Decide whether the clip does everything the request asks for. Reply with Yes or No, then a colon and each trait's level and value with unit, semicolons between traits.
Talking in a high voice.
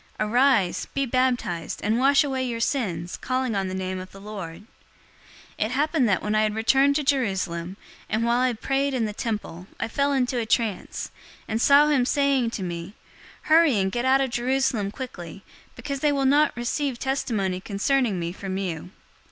Yes: high, 235 Hz